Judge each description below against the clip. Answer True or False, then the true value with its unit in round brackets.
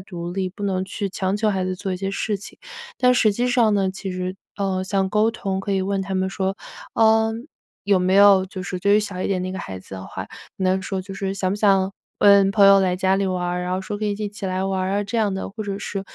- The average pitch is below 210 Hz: True (195 Hz)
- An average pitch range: False (1.4 semitones)